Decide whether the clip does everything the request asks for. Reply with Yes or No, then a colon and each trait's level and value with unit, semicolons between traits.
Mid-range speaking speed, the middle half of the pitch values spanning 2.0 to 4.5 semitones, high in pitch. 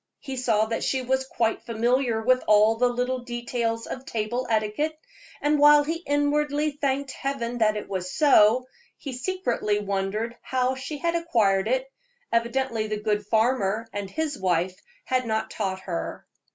Yes: average, 160 wpm; average, 3.9 semitones; high, 240 Hz